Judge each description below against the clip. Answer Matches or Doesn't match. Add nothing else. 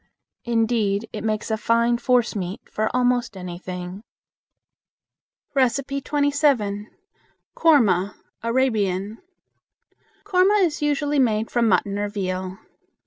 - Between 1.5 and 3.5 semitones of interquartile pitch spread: Doesn't match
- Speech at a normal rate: Doesn't match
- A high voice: Matches